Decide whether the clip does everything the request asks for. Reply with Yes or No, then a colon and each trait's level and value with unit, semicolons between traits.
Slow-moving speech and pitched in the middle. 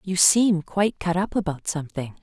No: average, 190 wpm; medium, 180 Hz